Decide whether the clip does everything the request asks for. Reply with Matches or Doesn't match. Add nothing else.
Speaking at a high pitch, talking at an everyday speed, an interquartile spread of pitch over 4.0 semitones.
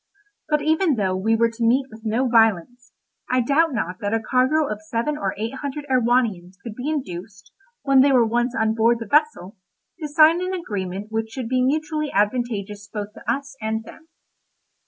Matches